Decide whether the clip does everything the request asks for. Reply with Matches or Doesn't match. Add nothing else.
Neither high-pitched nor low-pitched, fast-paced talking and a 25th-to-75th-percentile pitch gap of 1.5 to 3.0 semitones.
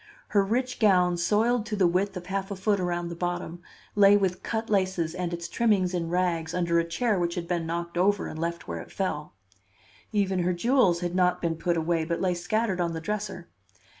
Matches